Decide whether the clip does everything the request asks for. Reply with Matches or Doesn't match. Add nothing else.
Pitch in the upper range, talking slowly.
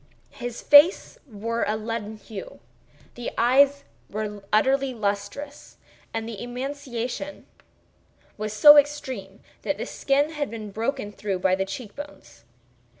Matches